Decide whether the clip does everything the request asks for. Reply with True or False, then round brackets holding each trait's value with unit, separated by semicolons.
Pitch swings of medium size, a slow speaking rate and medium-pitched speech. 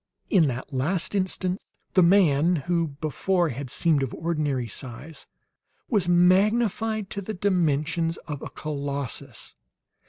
True (4.7 semitones; 125 wpm; 165 Hz)